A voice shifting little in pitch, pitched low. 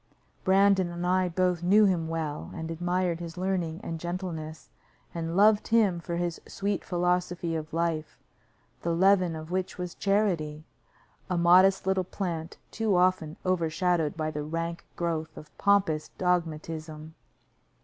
No: narrow, 2.3 semitones; medium, 175 Hz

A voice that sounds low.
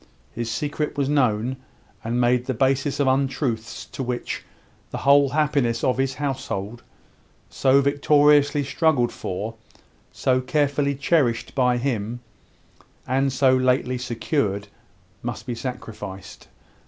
Yes: low, 130 Hz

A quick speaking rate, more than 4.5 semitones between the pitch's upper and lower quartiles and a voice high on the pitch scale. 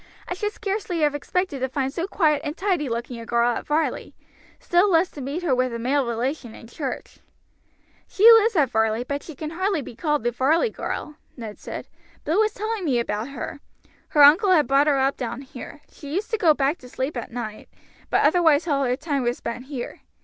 Yes: fast, 215 wpm; average, 5.3 semitones; very high, 285 Hz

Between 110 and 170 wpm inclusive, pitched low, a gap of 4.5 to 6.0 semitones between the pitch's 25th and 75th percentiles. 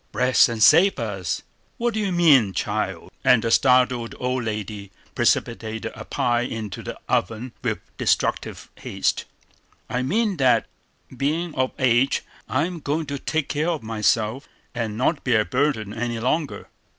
Yes: average, 150 wpm; low, 125 Hz; average, 4.8 semitones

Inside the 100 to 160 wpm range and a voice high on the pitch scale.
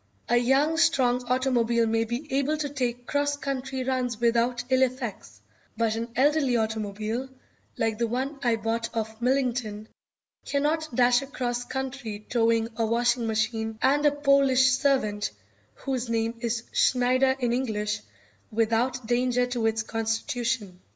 Yes: average, 140 wpm; high, 245 Hz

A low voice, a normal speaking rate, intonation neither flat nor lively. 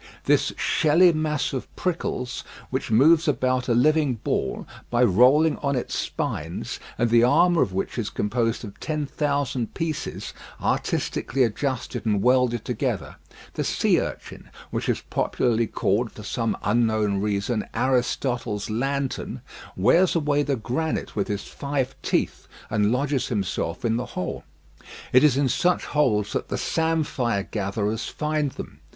Yes: low, 125 Hz; average, 145 wpm; average, 4.8 semitones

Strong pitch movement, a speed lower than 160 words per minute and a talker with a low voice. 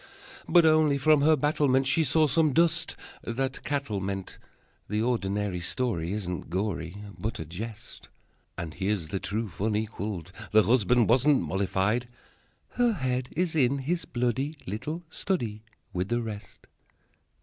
Yes: wide, 6.3 semitones; average, 140 wpm; low, 120 Hz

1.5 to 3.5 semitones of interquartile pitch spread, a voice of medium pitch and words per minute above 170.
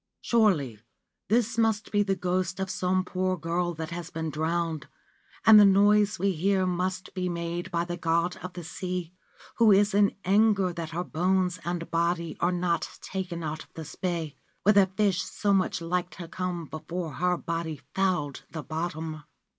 Yes: narrow, 2.4 semitones; medium, 180 Hz; average, 180 wpm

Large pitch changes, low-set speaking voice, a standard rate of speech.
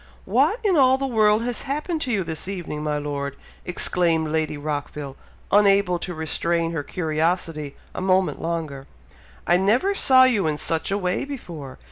No: wide, 5.7 semitones; medium, 175 Hz; average, 165 wpm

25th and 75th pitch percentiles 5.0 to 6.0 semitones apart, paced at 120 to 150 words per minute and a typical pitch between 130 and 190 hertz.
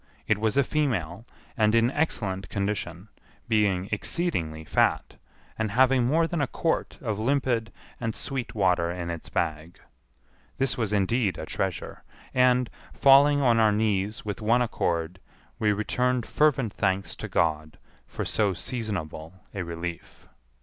No: wide, 5.5 semitones; average, 145 wpm; low, 105 Hz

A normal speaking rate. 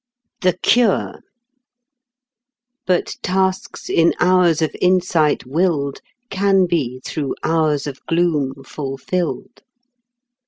No: slow, 90 wpm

